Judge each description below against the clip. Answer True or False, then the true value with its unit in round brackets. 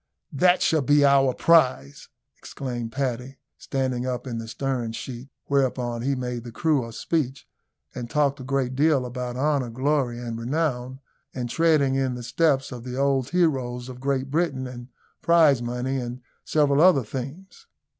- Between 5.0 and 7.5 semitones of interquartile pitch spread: False (2.5 semitones)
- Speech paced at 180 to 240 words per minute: False (165 wpm)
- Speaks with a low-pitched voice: True (130 Hz)